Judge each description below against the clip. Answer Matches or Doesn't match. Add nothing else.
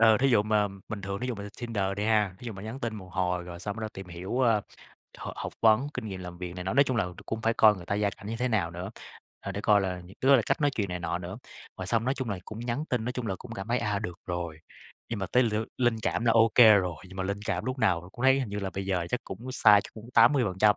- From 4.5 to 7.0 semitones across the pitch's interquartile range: Doesn't match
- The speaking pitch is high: Doesn't match